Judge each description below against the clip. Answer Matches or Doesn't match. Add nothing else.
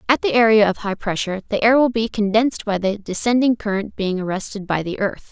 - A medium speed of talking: Doesn't match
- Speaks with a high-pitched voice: Matches